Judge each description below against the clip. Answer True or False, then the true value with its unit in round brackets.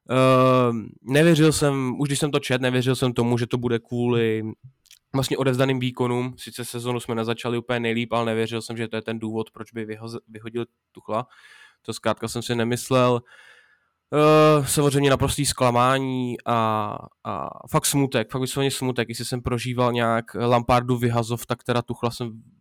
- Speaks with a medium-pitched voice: False (120 Hz)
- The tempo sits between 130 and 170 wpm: True (165 wpm)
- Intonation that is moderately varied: False (2.0 semitones)